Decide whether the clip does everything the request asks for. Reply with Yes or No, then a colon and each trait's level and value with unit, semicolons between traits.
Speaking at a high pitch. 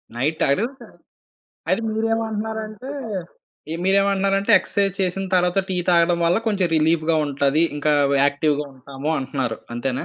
No: medium, 175 Hz